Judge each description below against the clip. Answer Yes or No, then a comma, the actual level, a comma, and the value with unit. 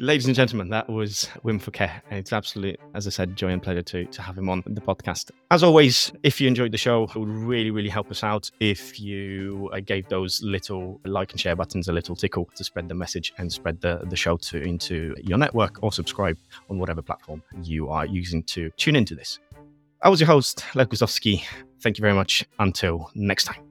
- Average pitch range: Yes, average, 3.6 semitones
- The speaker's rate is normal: No, fast, 220 wpm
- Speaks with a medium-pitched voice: No, low, 100 Hz